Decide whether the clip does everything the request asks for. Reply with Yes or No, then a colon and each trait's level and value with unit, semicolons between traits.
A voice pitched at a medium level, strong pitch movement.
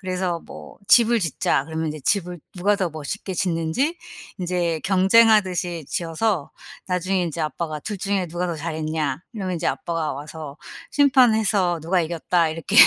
No: medium, 175 Hz; average, 3.3 semitones